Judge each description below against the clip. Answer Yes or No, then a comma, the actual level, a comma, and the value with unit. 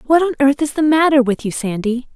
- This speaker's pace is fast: Yes, fast, 250 wpm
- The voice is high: Yes, very high, 275 Hz